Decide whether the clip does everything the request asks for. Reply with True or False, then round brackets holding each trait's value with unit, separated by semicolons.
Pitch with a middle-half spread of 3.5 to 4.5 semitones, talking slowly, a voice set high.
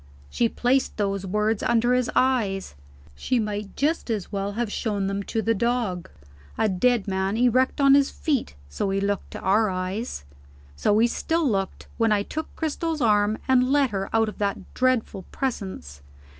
False (4.1 semitones; 175 wpm; 220 Hz)